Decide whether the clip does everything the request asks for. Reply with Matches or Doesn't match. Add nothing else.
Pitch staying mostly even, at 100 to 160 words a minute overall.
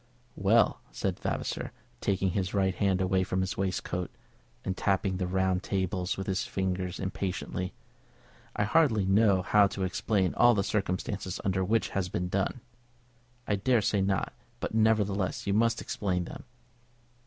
Matches